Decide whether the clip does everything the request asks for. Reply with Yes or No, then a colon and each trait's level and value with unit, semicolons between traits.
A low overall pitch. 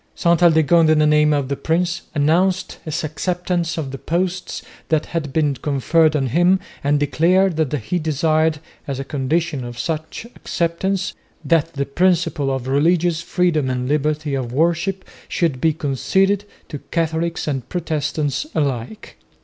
No: medium, 155 Hz